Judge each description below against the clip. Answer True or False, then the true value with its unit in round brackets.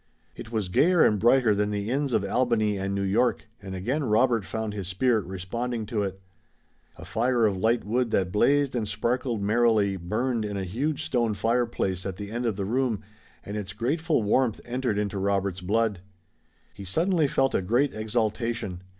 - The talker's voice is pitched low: True (110 Hz)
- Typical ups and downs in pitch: True (3.6 semitones)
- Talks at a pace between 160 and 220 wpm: True (185 wpm)